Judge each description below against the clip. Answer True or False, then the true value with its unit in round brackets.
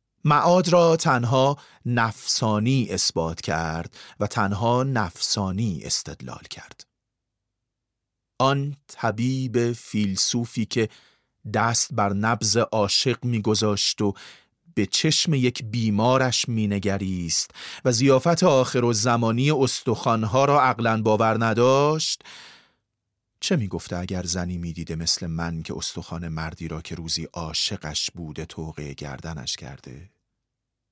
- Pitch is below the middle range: True (110 Hz)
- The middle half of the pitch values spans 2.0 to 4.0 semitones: False (5.2 semitones)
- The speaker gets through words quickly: False (105 wpm)